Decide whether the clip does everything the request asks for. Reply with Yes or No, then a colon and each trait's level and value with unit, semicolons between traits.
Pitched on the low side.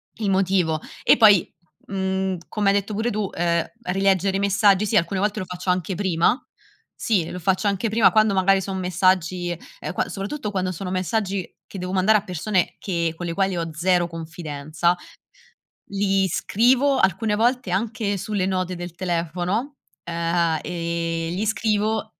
No: high, 190 Hz